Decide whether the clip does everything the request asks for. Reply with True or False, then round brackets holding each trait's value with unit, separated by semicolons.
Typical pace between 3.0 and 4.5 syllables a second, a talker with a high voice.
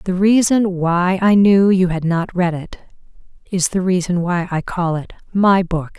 False (4.1 syllables/s; 180 Hz)